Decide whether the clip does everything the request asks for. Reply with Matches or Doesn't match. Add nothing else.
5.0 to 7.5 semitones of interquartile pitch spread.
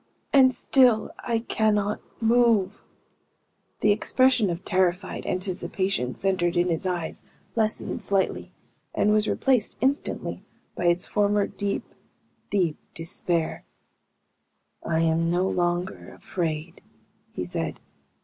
Doesn't match